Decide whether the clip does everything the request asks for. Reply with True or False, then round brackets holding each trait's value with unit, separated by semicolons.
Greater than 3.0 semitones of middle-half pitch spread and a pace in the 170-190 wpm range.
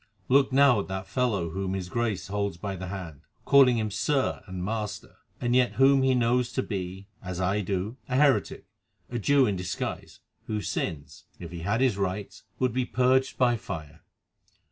True (5.2 semitones; 185 wpm)